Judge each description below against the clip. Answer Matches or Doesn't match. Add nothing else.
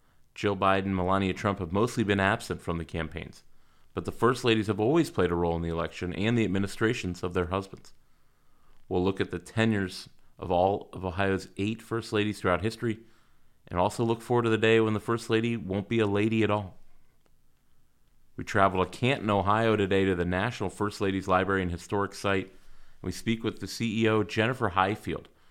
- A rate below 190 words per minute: Doesn't match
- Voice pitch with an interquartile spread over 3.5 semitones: Doesn't match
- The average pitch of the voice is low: Matches